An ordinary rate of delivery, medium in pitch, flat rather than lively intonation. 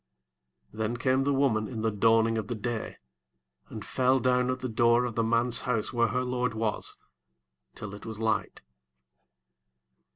No: average, 170 wpm; low, 115 Hz; narrow, 2.1 semitones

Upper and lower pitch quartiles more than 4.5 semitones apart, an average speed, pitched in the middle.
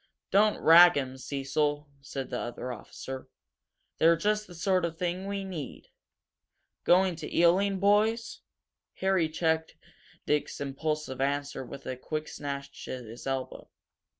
No: average, 5.1 semitones; slow, 125 wpm; medium, 155 Hz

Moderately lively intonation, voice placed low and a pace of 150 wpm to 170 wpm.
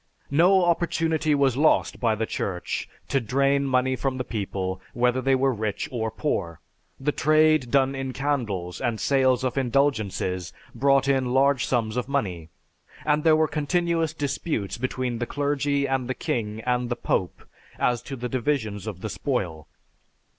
Yes: average, 4.1 semitones; low, 130 Hz; average, 160 wpm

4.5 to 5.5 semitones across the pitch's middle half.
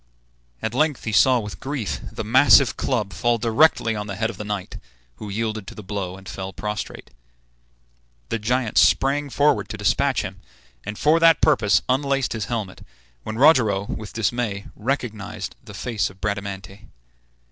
No: average, 3.9 semitones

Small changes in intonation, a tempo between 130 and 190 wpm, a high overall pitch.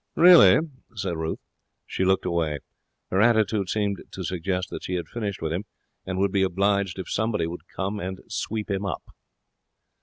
No: narrow, 2.1 semitones; average, 175 wpm; very low, 95 Hz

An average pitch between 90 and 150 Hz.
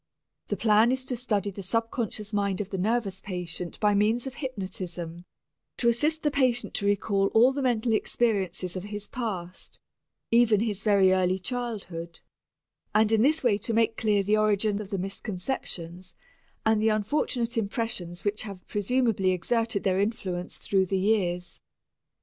No: high, 210 Hz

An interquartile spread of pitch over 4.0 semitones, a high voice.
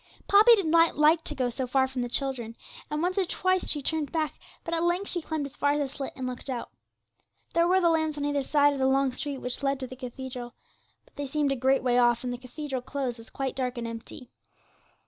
No: average, 3.7 semitones; very high, 275 Hz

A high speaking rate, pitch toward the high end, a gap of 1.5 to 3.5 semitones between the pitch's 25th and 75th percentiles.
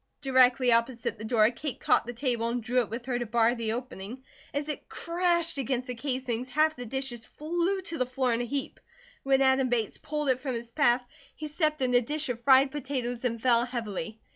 Yes: fast, 215 wpm; very high, 255 Hz; average, 2.8 semitones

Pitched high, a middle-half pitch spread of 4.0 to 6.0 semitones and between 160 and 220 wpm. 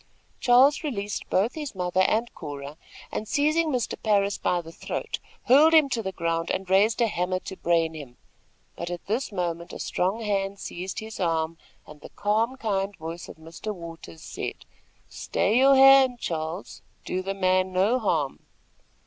Yes: high, 195 Hz; average, 5.3 semitones; average, 170 wpm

